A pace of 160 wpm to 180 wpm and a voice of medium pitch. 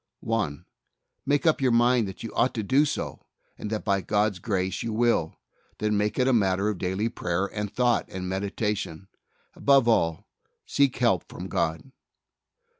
No: average, 170 wpm; low, 105 Hz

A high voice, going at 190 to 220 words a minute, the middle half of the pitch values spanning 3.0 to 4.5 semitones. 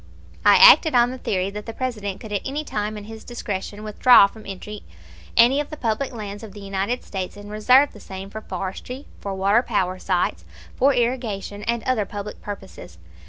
Yes: high, 210 Hz; average, 195 wpm; average, 3.5 semitones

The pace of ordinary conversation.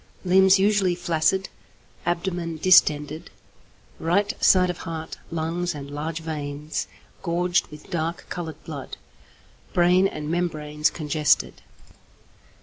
No: slow, 105 wpm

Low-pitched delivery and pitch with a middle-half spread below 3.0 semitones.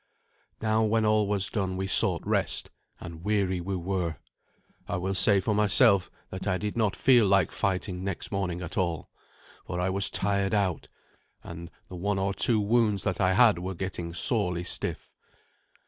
Yes: very low, 95 Hz; narrow, 2.4 semitones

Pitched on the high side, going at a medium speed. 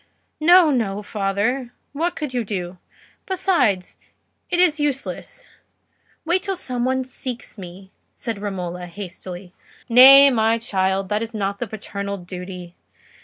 No: high, 220 Hz; slow, 130 wpm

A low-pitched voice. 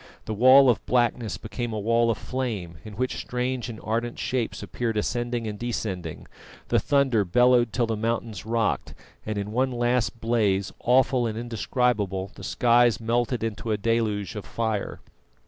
Yes: low, 115 Hz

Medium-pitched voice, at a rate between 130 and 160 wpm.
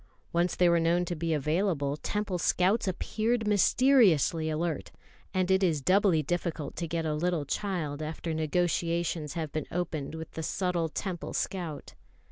Yes: medium, 170 Hz; average, 155 wpm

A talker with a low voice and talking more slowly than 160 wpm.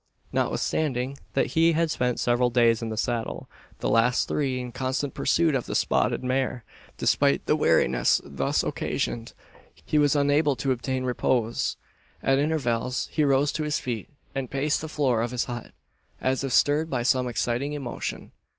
No: low, 130 Hz; average, 170 wpm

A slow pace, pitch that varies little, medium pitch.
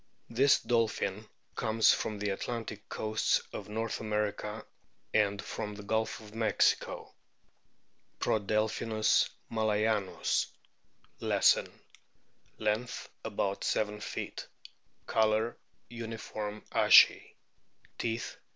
No: slow, 95 wpm; narrow, 1.1 semitones; low, 110 Hz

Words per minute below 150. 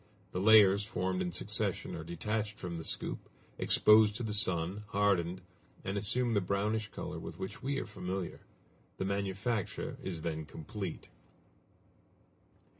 Yes: average, 140 wpm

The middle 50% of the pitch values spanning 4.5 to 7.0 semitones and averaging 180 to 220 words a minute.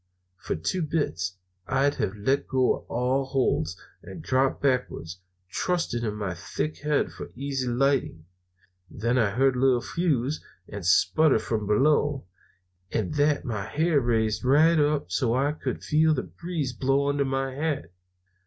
No: average, 4.8 semitones; average, 155 wpm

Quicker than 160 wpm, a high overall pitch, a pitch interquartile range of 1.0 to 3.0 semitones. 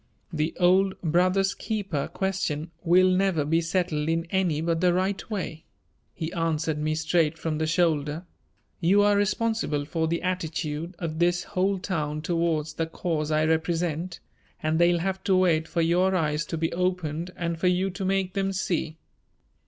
No: average, 170 wpm; medium, 170 Hz; average, 2.7 semitones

